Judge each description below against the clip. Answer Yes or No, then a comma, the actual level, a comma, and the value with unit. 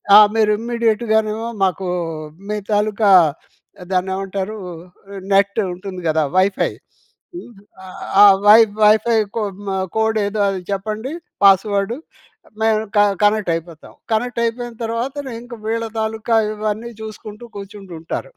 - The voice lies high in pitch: Yes, high, 215 Hz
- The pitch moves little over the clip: Yes, narrow, 2.2 semitones